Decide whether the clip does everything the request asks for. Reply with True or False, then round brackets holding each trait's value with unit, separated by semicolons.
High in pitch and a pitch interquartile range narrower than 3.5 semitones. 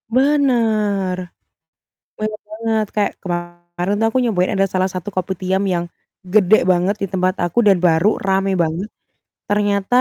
True (195 Hz; 2.8 semitones)